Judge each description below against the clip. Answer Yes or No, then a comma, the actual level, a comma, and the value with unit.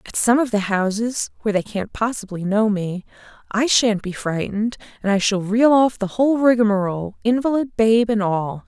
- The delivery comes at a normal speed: Yes, average, 175 wpm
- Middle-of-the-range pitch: No, high, 215 Hz